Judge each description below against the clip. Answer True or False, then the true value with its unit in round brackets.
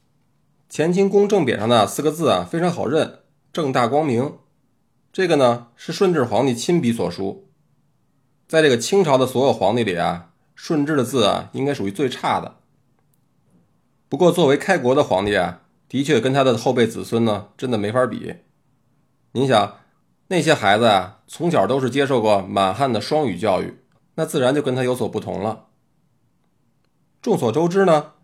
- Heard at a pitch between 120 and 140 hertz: True (135 Hz)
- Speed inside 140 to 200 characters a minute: False (250 characters per minute)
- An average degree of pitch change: True (4.9 semitones)